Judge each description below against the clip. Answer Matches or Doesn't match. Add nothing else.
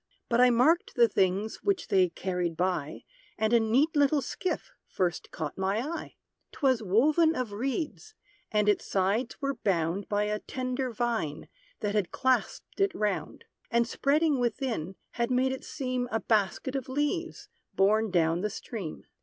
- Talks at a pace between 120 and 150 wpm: Doesn't match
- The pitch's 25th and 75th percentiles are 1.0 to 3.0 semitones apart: Doesn't match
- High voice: Matches